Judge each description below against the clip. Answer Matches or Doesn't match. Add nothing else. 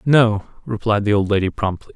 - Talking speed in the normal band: Matches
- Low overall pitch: Matches